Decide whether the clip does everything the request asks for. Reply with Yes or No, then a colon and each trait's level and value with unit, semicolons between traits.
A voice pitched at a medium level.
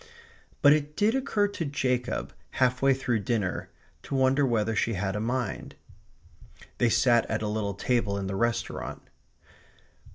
No: low, 120 Hz